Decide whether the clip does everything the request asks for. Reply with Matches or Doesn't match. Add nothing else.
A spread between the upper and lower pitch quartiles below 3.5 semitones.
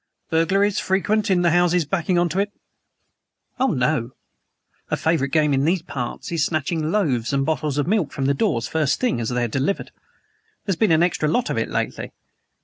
Doesn't match